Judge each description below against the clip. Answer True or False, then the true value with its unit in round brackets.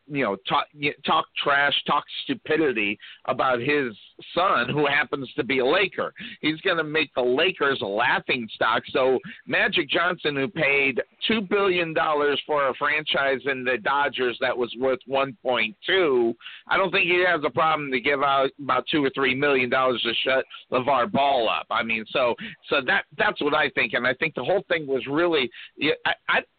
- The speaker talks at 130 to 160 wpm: False (190 wpm)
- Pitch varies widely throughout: False (3.3 semitones)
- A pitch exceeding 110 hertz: True (140 Hz)